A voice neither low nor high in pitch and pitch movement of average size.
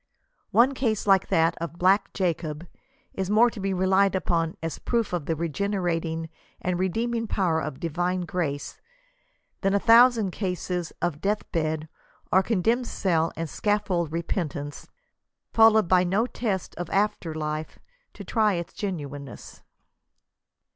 Yes: medium, 180 Hz; average, 4.0 semitones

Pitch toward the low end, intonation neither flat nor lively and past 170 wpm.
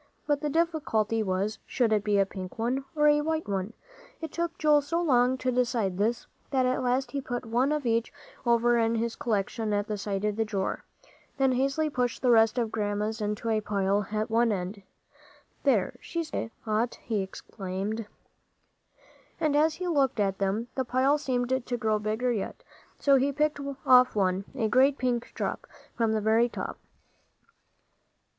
No: high, 235 Hz; average, 4.0 semitones; average, 180 wpm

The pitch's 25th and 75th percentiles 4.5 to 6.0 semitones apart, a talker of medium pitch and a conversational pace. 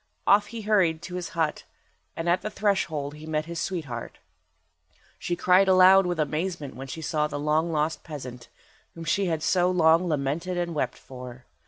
No: average, 3.3 semitones; medium, 165 Hz; average, 180 wpm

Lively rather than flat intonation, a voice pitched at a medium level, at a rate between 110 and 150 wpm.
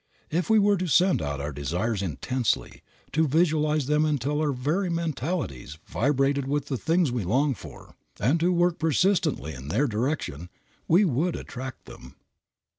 No: wide, 6.3 semitones; medium, 145 Hz; average, 160 wpm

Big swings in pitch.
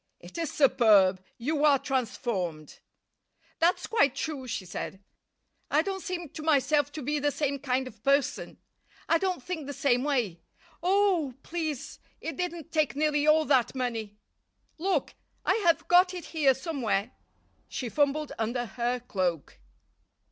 No: average, 4.7 semitones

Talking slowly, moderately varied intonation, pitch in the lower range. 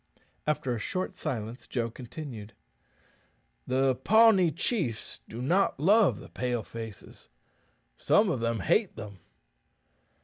No: slow, 115 wpm; wide, 7.6 semitones; low, 130 Hz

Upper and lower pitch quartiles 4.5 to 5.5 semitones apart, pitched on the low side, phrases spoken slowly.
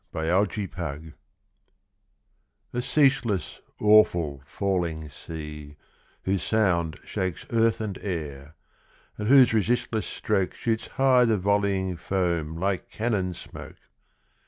Yes: average, 5.0 semitones; very low, 95 Hz; slow, 100 wpm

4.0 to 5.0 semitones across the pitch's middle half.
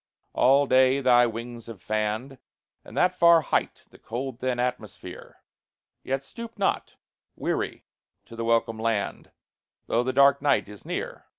No: average, 3.1 semitones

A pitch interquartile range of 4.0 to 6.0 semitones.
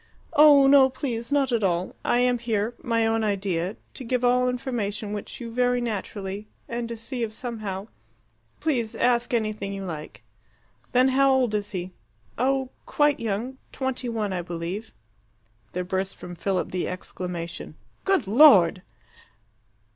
Yes: average, 4.3 semitones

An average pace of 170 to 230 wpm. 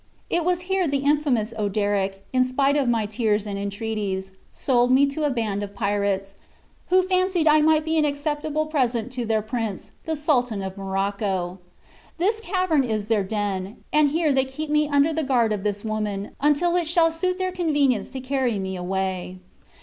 Yes: average, 185 wpm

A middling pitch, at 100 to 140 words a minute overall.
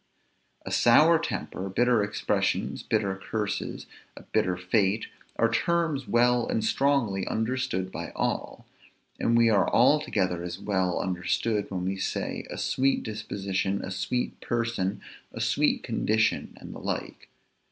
No: low, 110 Hz; slow, 135 wpm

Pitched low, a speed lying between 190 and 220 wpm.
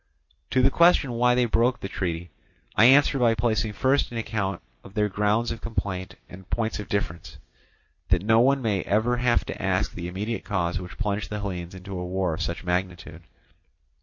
Yes: low, 105 Hz; average, 195 wpm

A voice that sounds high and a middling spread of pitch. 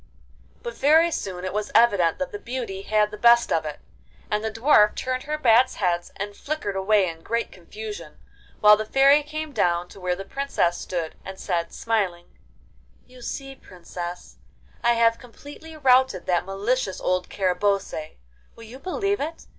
No: high, 210 Hz; wide, 6.0 semitones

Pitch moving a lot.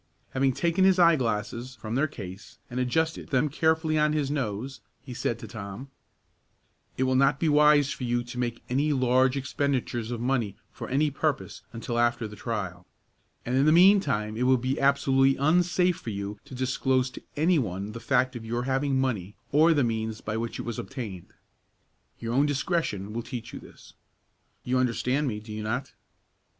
No: average, 3.7 semitones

